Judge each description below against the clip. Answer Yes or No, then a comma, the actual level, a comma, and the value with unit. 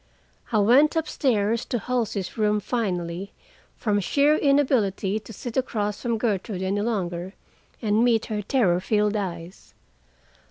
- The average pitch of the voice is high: Yes, high, 210 Hz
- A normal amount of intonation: Yes, average, 3.6 semitones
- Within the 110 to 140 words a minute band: Yes, slow, 135 wpm